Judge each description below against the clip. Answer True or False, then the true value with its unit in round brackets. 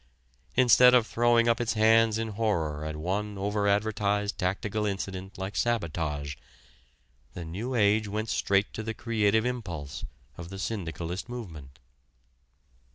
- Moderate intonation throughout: True (3.7 semitones)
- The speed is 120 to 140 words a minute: True (135 wpm)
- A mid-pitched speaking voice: False (105 Hz)